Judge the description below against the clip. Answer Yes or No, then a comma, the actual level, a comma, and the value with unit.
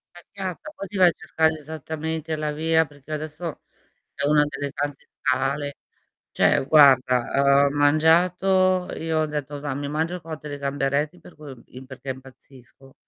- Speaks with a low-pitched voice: No, medium, 150 Hz